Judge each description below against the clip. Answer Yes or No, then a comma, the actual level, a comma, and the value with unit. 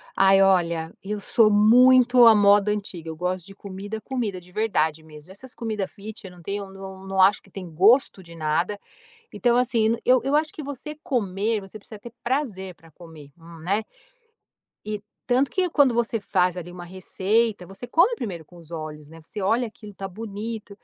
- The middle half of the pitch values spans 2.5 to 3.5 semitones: No, average, 4.1 semitones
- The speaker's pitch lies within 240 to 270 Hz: No, high, 200 Hz